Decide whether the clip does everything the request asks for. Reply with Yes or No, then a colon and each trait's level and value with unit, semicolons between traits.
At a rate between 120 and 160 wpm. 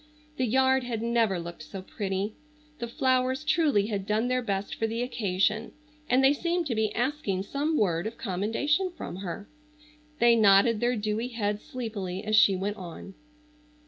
No: average, 170 wpm